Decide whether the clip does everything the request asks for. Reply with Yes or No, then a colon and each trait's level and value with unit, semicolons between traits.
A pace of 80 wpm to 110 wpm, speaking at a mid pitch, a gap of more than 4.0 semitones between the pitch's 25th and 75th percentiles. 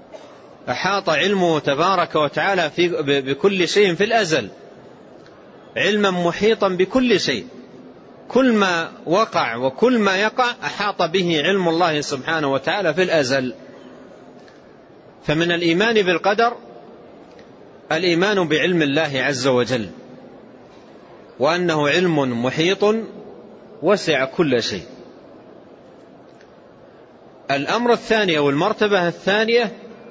Yes: average, 90 wpm; medium, 180 Hz; average, 5.1 semitones